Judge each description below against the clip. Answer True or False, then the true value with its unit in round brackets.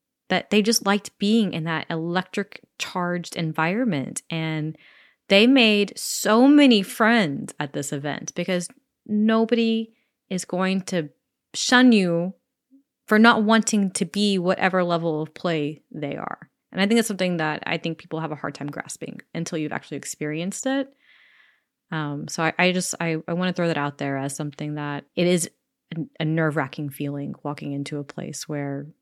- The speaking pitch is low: False (180 Hz)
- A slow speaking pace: False (170 wpm)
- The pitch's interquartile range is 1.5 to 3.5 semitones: False (5.4 semitones)